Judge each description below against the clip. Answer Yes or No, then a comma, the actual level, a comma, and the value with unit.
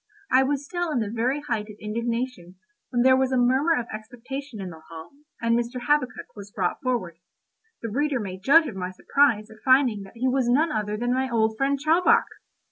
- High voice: Yes, high, 245 Hz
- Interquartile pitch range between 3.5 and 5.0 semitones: Yes, average, 4.1 semitones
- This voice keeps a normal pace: No, fast, 210 wpm